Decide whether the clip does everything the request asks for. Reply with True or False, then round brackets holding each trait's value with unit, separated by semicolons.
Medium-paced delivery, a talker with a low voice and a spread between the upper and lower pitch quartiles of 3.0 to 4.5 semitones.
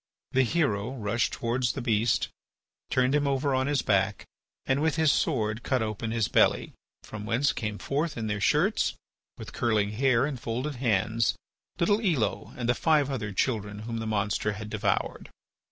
True (170 wpm; 115 Hz; 4.1 semitones)